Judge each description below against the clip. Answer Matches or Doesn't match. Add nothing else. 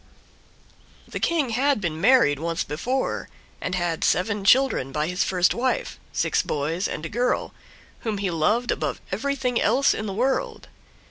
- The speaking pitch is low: Doesn't match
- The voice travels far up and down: Matches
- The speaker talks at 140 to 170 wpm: Matches